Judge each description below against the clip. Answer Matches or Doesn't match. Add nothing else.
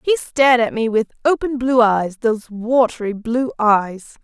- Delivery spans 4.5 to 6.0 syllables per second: Matches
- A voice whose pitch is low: Doesn't match